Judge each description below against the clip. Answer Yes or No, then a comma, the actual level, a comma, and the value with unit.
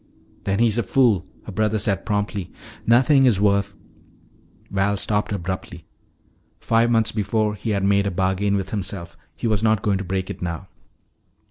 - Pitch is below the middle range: Yes, low, 100 Hz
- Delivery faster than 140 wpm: Yes, average, 170 wpm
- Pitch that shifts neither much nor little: No, narrow, 2.2 semitones